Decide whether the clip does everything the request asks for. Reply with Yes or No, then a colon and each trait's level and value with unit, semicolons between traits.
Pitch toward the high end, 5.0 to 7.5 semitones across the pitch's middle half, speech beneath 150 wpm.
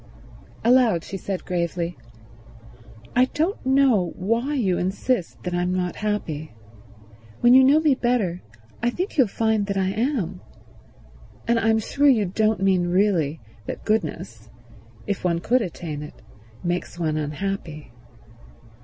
Yes: high, 195 Hz; wide, 5.5 semitones; slow, 135 wpm